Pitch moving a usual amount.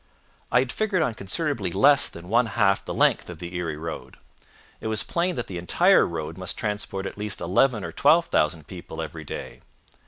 No: wide, 6.4 semitones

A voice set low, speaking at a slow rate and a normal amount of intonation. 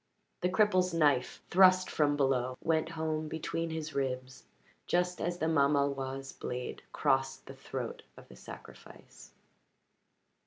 No: medium, 145 Hz; slow, 125 wpm; average, 3.9 semitones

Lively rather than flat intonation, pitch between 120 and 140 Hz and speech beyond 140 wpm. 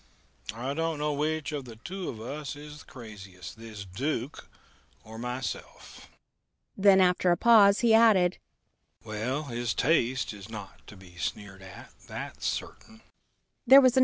No: wide, 7.1 semitones; low, 135 Hz; slow, 135 wpm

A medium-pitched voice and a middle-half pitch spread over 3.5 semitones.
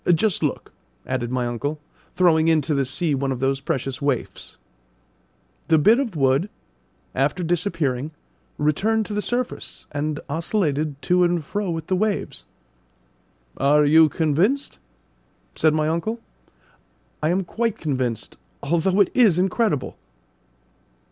Yes: medium, 160 Hz; average, 5.1 semitones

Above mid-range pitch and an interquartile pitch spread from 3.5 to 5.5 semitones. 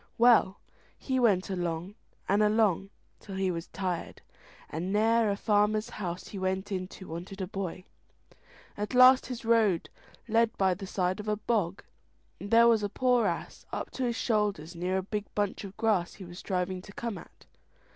No: high, 200 Hz; average, 3.1 semitones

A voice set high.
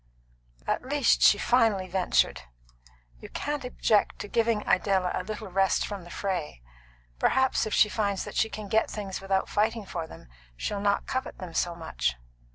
Yes: high, 200 Hz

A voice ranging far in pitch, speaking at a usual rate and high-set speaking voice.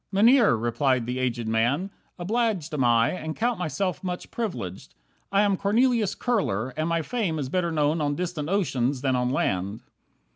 No: wide, 7.8 semitones; average, 170 wpm; medium, 160 Hz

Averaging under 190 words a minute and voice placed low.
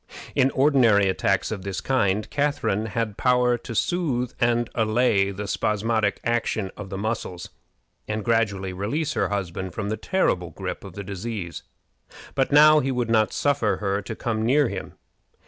Yes: average, 165 wpm; low, 110 Hz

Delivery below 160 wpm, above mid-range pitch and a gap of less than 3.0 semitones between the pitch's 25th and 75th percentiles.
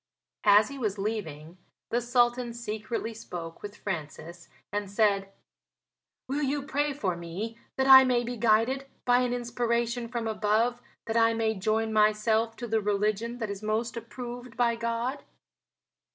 Yes: average, 150 wpm; high, 225 Hz; narrow, 2.5 semitones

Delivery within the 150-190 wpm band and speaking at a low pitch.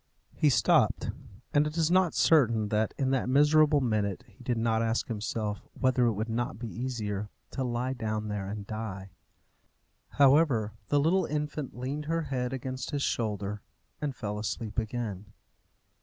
Yes: average, 160 wpm; low, 120 Hz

